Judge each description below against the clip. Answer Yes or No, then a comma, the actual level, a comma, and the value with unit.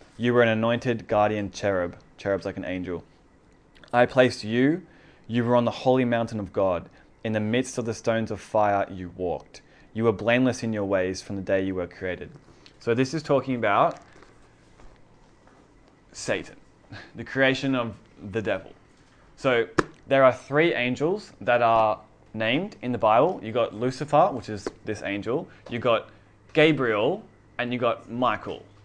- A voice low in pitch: Yes, low, 115 Hz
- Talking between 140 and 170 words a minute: Yes, average, 165 wpm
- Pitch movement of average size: Yes, average, 3.5 semitones